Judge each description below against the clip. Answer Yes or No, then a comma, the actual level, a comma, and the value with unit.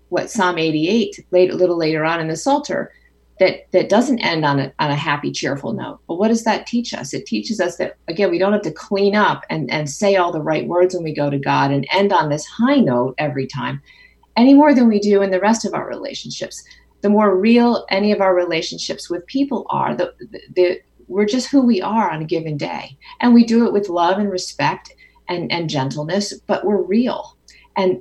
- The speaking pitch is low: No, medium, 185 Hz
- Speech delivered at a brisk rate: Yes, fast, 230 wpm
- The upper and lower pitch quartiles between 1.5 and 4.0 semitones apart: No, average, 4.9 semitones